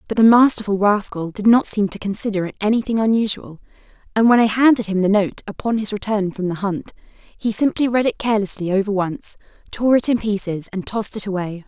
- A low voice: No, high, 210 Hz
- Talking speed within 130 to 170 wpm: No, fast, 205 wpm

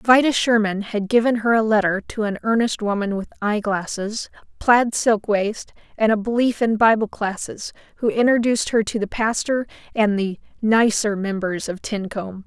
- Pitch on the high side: Yes, high, 215 Hz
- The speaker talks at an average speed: Yes, average, 170 wpm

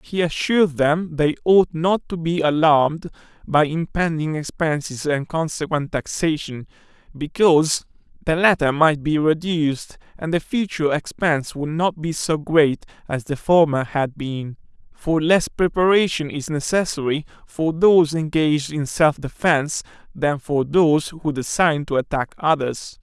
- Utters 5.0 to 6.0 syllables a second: No, 4.5 syllables/s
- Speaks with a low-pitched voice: No, medium, 155 Hz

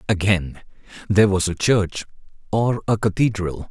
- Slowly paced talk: Yes, slow, 130 wpm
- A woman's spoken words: No, male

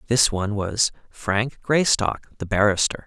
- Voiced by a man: Yes, male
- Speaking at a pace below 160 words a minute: Yes, slow, 135 wpm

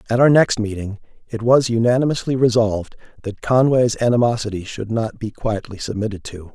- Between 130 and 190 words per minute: Yes, average, 155 wpm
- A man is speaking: Yes, male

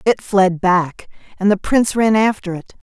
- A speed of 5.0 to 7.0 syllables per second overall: No, 4.6 syllables/s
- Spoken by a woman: Yes, female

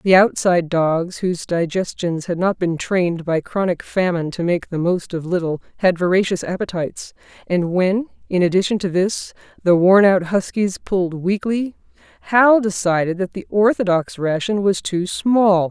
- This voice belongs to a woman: Yes, female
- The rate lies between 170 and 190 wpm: No, average, 160 wpm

